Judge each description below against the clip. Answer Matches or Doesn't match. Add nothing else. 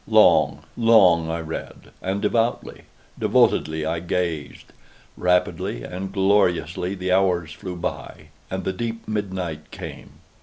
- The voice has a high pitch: Doesn't match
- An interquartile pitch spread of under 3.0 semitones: Matches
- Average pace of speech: Doesn't match